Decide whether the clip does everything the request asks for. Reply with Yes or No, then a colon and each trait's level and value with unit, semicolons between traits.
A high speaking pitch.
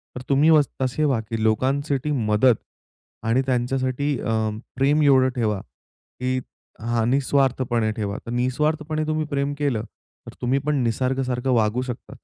No: low, 130 Hz